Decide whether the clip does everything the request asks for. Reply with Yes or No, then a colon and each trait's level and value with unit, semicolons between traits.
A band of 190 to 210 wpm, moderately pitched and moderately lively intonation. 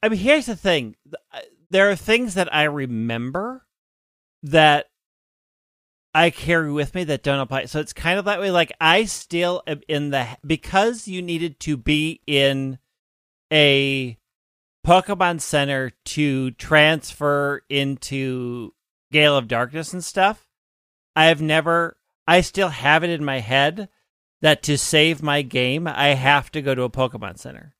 No: average, 155 wpm; medium, 150 Hz; average, 4.1 semitones